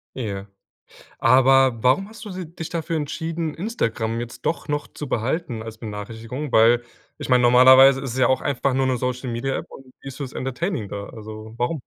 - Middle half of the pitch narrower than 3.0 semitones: No, average, 4.1 semitones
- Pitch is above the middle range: No, low, 130 Hz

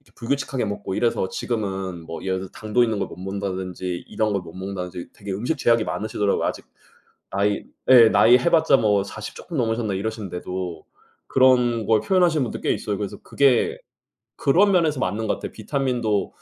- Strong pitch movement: No, average, 4.4 semitones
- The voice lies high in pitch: No, low, 110 Hz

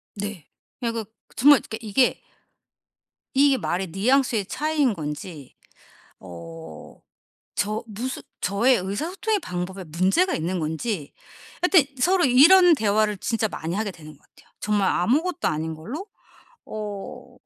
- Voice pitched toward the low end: No, high, 210 Hz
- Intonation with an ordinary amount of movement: No, wide, 7.0 semitones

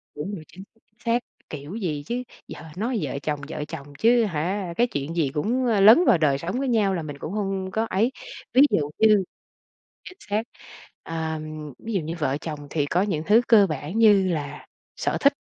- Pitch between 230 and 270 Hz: No, high, 190 Hz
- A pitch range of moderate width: No, wide, 6.3 semitones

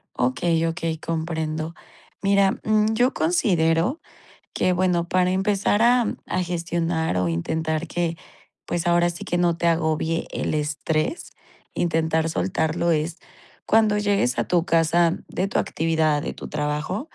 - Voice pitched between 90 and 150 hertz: No, medium, 170 Hz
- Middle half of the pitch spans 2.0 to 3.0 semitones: Yes, narrow, 2.6 semitones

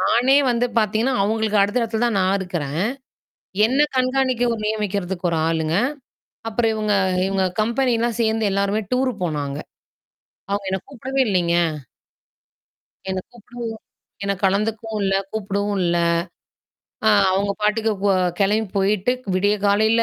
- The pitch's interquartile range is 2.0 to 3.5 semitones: Yes, average, 3.0 semitones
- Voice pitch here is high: Yes, high, 210 Hz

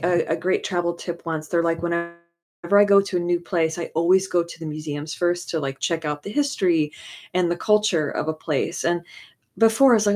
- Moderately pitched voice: Yes, medium, 170 Hz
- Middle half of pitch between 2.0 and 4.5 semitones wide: Yes, narrow, 2.6 semitones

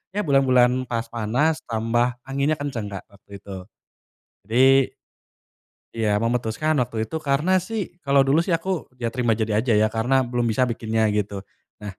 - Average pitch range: Yes, average, 3.8 semitones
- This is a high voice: No, low, 120 Hz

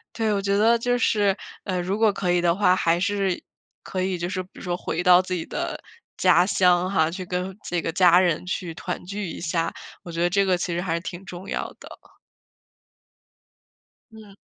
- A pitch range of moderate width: No, narrow, 2.1 semitones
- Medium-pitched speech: Yes, medium, 180 Hz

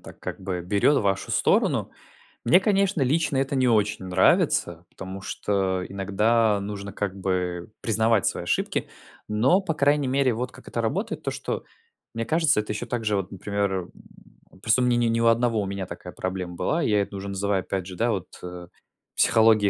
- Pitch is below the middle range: Yes, low, 105 Hz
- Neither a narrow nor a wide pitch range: Yes, average, 3.9 semitones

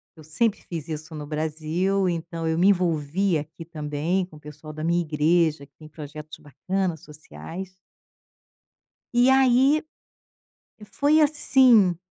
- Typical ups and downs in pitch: Yes, average, 3.9 semitones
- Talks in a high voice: No, medium, 165 Hz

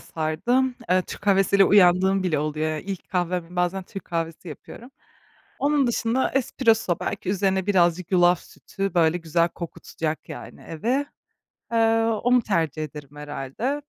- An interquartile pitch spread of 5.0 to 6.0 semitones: Yes, average, 5.3 semitones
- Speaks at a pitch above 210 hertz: No, medium, 185 Hz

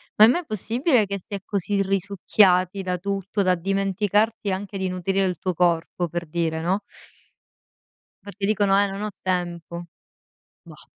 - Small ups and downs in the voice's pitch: Yes, narrow, 2.1 semitones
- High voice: Yes, high, 195 Hz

